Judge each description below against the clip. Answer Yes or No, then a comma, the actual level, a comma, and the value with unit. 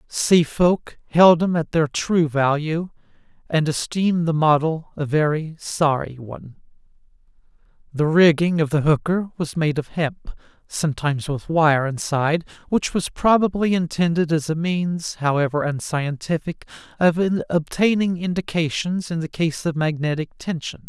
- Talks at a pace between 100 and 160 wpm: Yes, slow, 135 wpm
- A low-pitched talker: No, medium, 160 Hz